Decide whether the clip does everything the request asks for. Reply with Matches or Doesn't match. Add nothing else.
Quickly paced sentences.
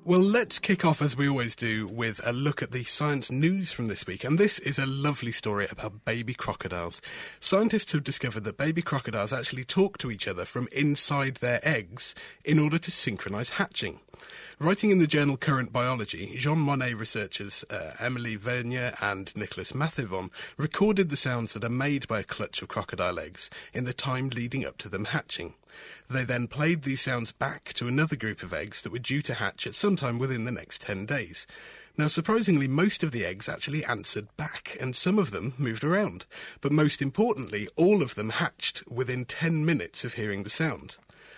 Doesn't match